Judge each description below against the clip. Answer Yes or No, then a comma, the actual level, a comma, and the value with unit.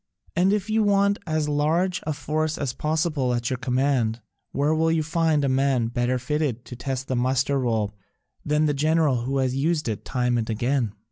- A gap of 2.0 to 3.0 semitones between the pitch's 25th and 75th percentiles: No, average, 4.1 semitones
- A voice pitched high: No, medium, 140 Hz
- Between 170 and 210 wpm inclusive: Yes, average, 195 wpm